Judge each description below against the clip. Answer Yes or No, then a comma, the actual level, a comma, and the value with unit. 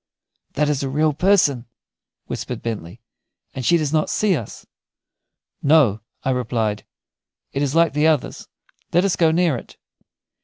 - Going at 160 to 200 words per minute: No, average, 150 wpm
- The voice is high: No, medium, 145 Hz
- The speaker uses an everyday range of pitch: Yes, average, 4.4 semitones